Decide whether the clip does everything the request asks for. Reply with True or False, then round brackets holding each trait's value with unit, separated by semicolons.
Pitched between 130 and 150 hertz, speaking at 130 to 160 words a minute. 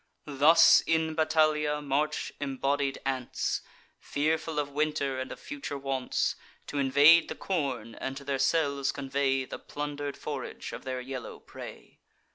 True (140 Hz; 140 wpm)